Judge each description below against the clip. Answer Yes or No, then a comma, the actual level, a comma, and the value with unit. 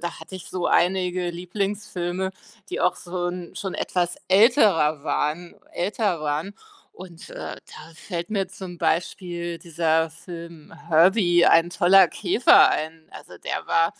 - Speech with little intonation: Yes, narrow, 2.1 semitones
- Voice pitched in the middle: Yes, medium, 175 Hz